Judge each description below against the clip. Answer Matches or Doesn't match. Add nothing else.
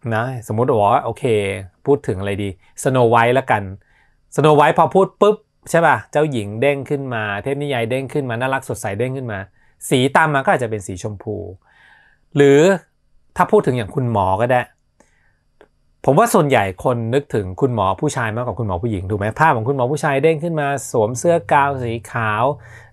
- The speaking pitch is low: Matches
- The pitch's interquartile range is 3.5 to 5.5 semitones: Matches